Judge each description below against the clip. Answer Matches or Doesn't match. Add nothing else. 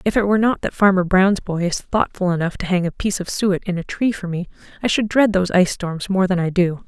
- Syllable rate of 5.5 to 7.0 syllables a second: Matches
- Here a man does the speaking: Doesn't match